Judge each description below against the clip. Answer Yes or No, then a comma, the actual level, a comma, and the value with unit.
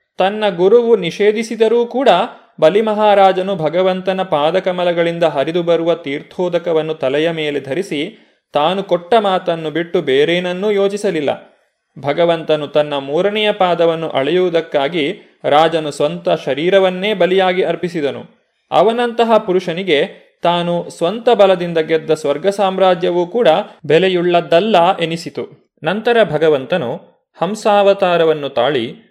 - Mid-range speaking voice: Yes, medium, 175 Hz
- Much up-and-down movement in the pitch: No, average, 3.6 semitones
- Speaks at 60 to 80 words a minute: No, average, 90 wpm